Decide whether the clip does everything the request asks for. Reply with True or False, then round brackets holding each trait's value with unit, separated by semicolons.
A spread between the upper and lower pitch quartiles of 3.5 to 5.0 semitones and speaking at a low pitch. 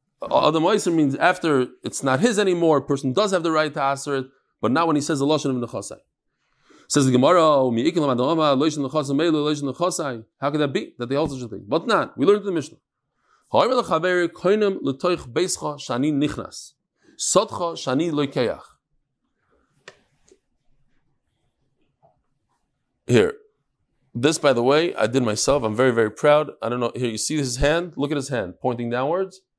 False (4.4 semitones; 145 Hz)